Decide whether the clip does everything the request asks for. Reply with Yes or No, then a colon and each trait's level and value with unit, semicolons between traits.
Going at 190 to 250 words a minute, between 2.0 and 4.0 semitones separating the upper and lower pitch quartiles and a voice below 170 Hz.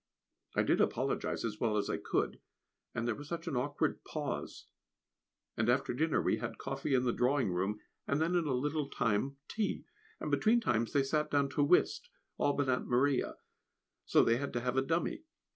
Yes: average, 195 wpm; average, 3.5 semitones; low, 135 Hz